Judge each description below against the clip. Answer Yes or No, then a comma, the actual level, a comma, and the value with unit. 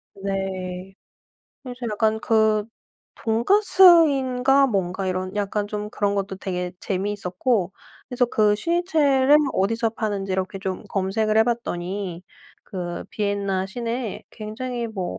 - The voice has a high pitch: Yes, high, 210 Hz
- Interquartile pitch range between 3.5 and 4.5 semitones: Yes, average, 3.9 semitones